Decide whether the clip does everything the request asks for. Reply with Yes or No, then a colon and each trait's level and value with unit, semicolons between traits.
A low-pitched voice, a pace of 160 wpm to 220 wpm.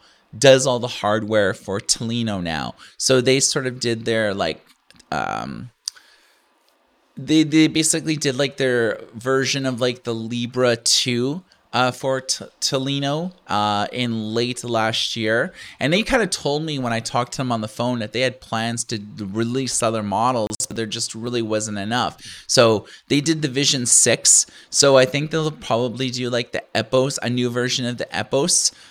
Yes: low, 125 Hz; average, 175 wpm